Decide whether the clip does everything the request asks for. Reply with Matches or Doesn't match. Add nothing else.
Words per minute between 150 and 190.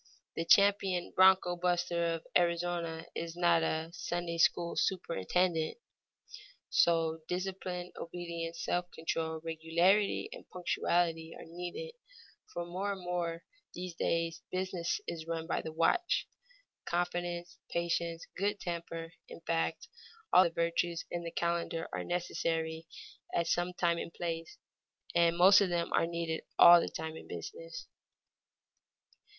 Doesn't match